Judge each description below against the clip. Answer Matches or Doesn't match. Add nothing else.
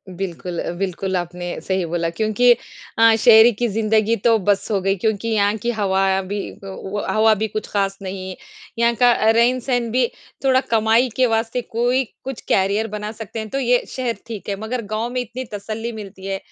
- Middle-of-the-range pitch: Doesn't match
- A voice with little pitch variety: Doesn't match